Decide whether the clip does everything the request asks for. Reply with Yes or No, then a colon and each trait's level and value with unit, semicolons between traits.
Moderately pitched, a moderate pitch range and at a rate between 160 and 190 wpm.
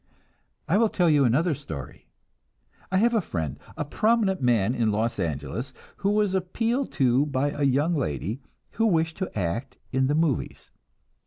No: medium, 145 Hz; wide, 8.0 semitones; average, 165 wpm